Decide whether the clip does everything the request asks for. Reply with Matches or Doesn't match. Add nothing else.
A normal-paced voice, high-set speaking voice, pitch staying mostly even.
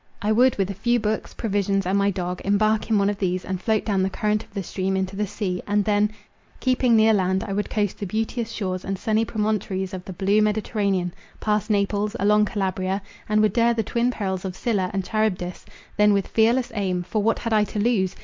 Doesn't match